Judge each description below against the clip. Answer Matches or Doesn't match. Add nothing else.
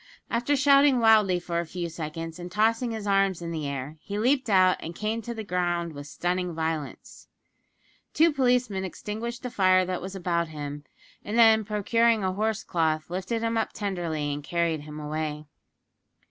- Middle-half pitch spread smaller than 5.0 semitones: Doesn't match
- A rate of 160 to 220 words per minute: Matches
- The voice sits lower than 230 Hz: Matches